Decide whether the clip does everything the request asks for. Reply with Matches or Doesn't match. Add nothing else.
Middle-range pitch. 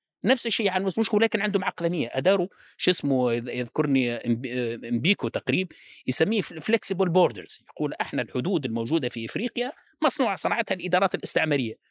Matches